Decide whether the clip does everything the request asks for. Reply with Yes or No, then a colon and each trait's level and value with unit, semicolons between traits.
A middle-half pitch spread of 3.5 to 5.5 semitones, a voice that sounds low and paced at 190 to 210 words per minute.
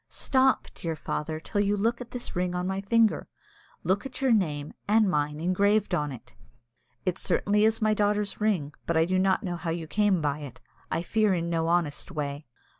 No: average, 4.5 semitones; medium, 185 Hz; average, 200 wpm